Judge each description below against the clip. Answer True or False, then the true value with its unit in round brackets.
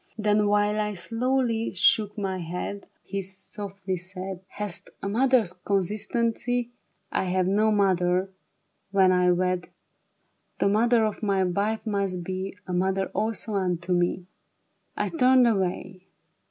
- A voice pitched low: False (195 Hz)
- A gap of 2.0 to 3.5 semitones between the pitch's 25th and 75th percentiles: True (2.7 semitones)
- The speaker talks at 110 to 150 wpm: True (140 wpm)